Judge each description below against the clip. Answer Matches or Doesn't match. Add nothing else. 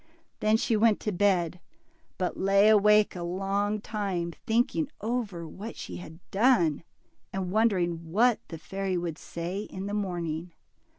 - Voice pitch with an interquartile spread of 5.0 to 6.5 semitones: Doesn't match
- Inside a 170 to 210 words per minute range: Doesn't match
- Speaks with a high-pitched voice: Matches